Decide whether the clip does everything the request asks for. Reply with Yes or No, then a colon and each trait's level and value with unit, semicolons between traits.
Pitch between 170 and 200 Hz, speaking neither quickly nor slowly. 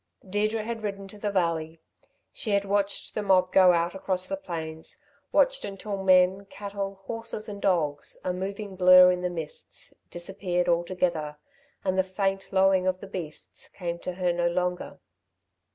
Yes: medium, 185 Hz; average, 165 wpm